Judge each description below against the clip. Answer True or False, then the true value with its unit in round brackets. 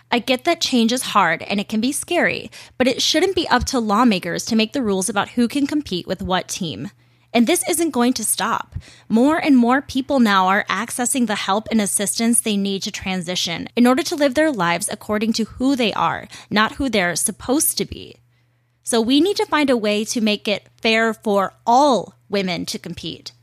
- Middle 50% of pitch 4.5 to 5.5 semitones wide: True (4.8 semitones)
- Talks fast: True (215 wpm)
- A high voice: True (225 Hz)